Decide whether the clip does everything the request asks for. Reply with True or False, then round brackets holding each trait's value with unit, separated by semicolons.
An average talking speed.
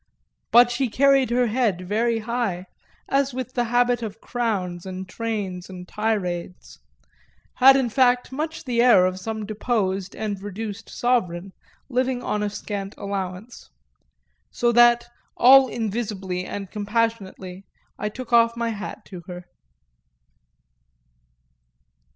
False (125 wpm)